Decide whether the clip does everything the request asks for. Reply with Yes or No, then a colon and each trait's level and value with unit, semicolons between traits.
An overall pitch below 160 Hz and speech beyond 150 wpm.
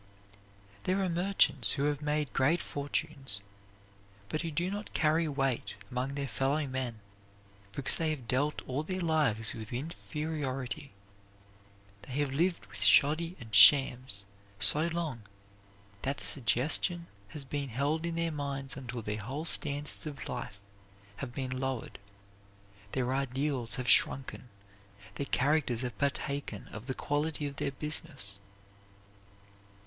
No: medium, 140 Hz; slow, 135 wpm